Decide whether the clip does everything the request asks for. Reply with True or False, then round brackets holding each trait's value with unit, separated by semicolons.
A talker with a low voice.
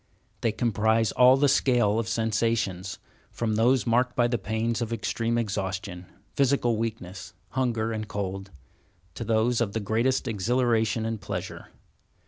True (115 Hz)